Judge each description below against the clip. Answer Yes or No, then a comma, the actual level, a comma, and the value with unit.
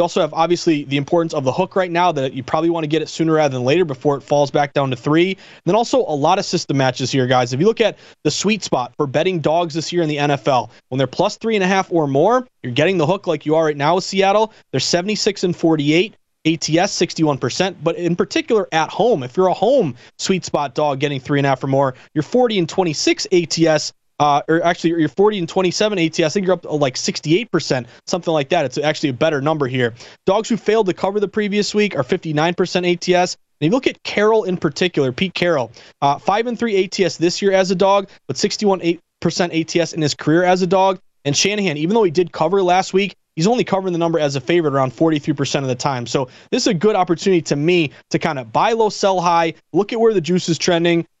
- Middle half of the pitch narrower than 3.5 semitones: No, average, 4.2 semitones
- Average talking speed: No, fast, 245 wpm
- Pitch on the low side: No, medium, 170 Hz